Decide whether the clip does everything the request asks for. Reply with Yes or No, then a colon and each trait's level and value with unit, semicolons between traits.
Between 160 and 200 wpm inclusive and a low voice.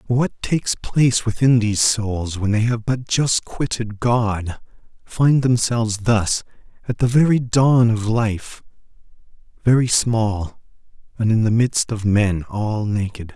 No: average, 145 wpm; low, 115 Hz